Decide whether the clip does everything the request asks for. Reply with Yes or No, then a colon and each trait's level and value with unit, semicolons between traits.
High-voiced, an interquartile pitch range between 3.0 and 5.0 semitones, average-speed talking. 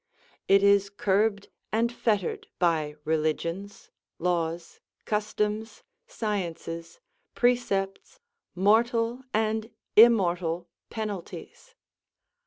No: high, 200 Hz; average, 4.1 semitones; slow, 70 wpm